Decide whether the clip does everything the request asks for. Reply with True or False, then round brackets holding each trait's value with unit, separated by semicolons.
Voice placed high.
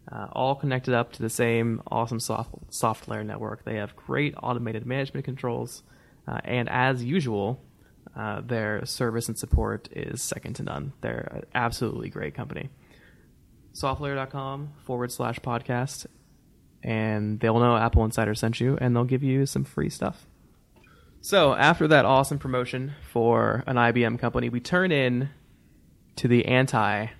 False (120 Hz)